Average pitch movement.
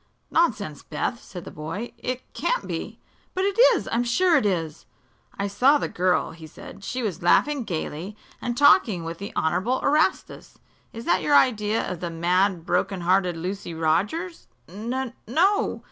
No: wide, 6.7 semitones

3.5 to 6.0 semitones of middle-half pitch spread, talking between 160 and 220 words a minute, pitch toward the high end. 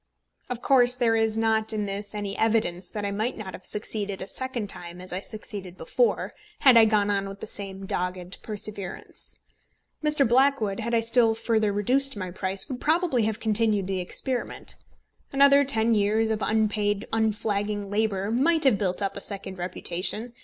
No: average, 2.8 semitones; average, 175 wpm; high, 215 Hz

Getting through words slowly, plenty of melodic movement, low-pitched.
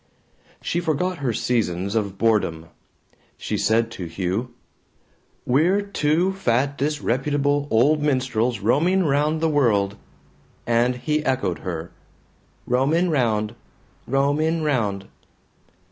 Yes: slow, 105 wpm; wide, 5.7 semitones; low, 130 Hz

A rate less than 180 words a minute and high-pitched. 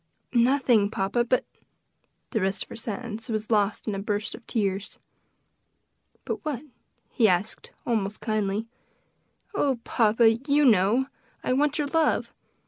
Yes: average, 140 wpm; high, 225 Hz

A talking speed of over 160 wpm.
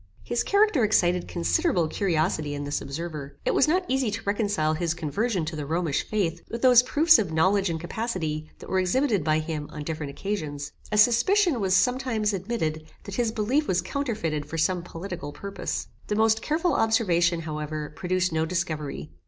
Yes: average, 175 wpm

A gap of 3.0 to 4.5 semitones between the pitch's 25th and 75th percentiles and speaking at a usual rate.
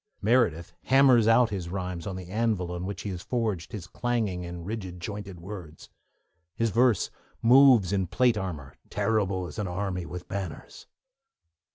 Yes: average, 4.2 semitones; average, 160 wpm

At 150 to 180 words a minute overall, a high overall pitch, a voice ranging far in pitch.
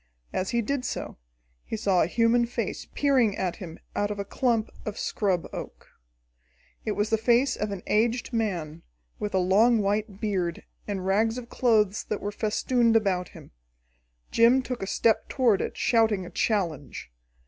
No: average, 170 wpm; high, 215 Hz; average, 3.3 semitones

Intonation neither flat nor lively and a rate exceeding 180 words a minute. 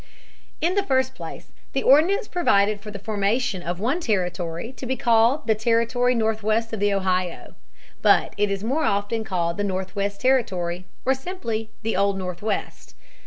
No: average, 4.1 semitones; average, 165 wpm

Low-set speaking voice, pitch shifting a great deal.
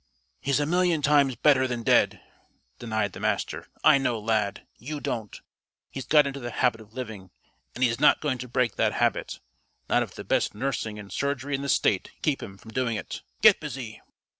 No: low, 125 Hz; average, 4.0 semitones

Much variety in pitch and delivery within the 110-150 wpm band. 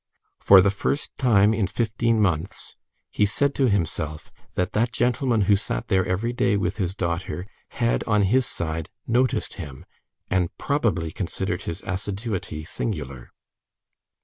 No: average, 4.8 semitones; average, 145 wpm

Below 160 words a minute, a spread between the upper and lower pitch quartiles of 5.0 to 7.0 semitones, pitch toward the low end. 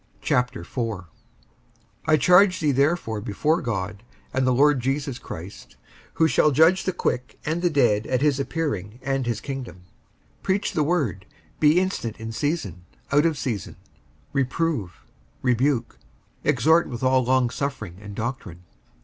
Yes: average, 140 wpm; average, 5.3 semitones; low, 130 Hz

